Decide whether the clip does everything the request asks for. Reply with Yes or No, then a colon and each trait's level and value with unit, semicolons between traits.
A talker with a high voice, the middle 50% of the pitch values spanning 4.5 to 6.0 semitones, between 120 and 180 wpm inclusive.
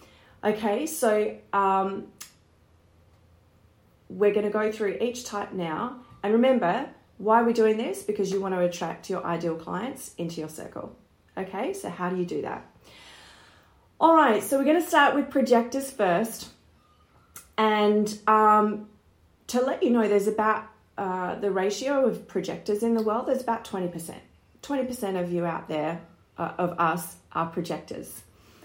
Yes: high, 210 Hz; average, 4.9 semitones; average, 155 wpm